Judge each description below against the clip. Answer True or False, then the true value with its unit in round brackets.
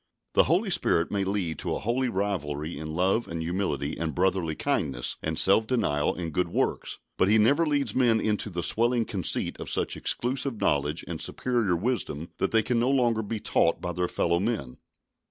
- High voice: False (95 Hz)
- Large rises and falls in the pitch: True (6.0 semitones)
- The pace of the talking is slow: False (190 wpm)